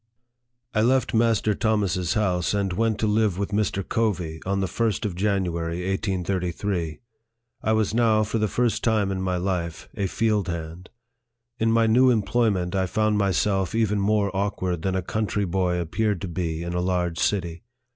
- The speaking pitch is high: No, low, 100 Hz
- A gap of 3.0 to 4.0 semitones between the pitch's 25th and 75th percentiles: Yes, average, 3.3 semitones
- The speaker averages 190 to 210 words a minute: No, average, 175 wpm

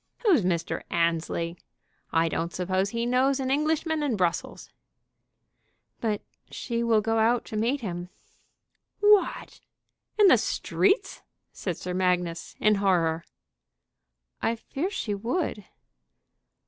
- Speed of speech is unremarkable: No, slow, 120 wpm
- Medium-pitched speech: No, high, 215 Hz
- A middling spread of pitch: No, wide, 7.0 semitones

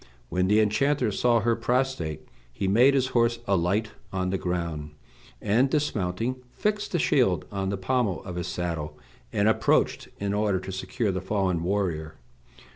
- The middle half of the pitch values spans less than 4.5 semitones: No, average, 4.8 semitones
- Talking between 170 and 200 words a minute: No, average, 160 wpm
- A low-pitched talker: Yes, low, 100 Hz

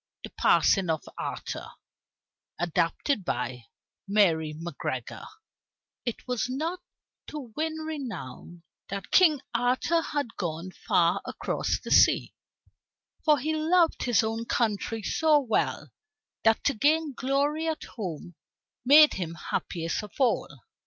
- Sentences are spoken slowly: Yes, slow, 120 wpm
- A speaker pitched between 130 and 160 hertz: No, high, 235 Hz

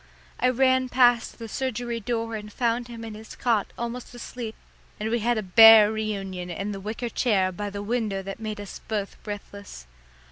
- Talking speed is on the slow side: No, average, 185 wpm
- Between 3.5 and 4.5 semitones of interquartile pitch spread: No, average, 2.7 semitones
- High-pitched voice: Yes, high, 220 Hz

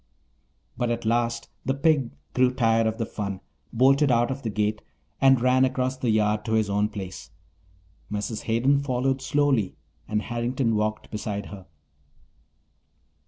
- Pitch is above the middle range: No, low, 115 Hz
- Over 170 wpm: No, average, 150 wpm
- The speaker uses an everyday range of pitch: Yes, average, 3.3 semitones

